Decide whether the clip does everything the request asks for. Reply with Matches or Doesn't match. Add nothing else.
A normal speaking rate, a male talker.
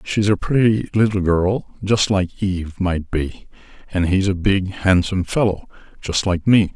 Matches